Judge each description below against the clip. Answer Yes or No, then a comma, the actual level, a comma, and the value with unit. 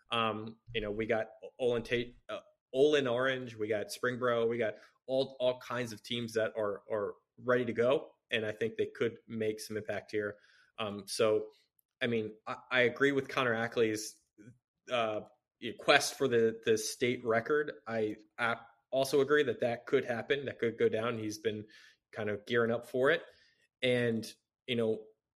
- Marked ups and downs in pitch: No, narrow, 2.6 semitones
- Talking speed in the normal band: Yes, average, 180 wpm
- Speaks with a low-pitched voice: Yes, low, 115 Hz